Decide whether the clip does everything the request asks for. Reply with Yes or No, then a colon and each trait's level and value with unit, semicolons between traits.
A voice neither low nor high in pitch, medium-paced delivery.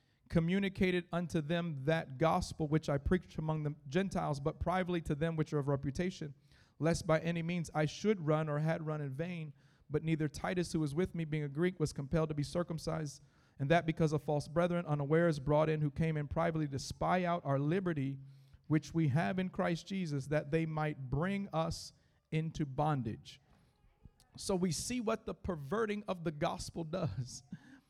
Yes: medium, 160 Hz; average, 185 wpm